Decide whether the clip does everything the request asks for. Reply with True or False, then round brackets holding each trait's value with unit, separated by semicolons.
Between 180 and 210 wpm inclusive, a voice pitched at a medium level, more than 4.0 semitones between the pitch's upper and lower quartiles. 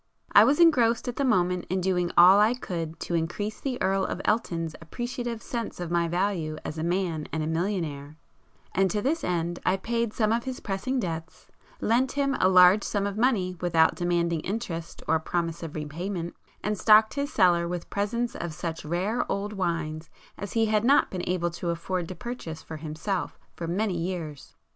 True (190 wpm; 180 Hz; 4.4 semitones)